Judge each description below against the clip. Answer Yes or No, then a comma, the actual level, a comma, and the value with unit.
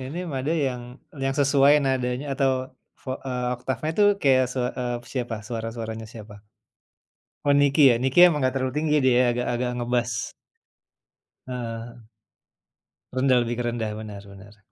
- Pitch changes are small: Yes, narrow, 2.3 semitones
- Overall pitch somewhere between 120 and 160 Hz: Yes, low, 125 Hz